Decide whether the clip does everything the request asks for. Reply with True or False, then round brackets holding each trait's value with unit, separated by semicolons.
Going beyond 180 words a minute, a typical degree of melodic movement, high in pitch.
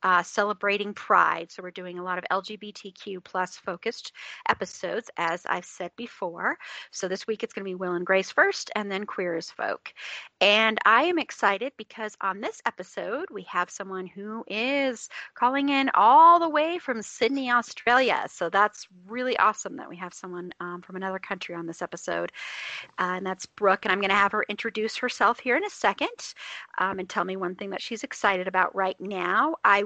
True (195 wpm; 4.1 semitones; 200 Hz)